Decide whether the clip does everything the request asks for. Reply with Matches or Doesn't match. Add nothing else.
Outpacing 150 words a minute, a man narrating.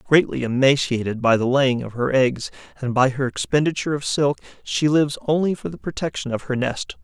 Matches